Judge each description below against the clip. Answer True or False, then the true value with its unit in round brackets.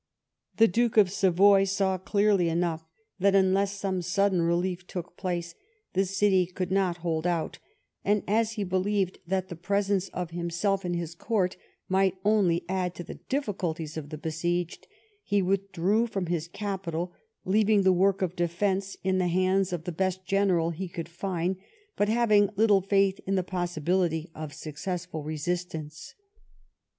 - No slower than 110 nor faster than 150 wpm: False (160 wpm)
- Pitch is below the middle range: False (185 Hz)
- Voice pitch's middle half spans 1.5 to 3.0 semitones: True (2.4 semitones)